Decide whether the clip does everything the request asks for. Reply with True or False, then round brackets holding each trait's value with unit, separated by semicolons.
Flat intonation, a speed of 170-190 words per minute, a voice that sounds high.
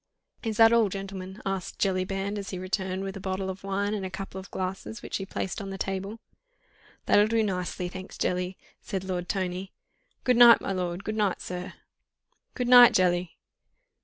True (1.7 semitones; 185 wpm; 195 Hz)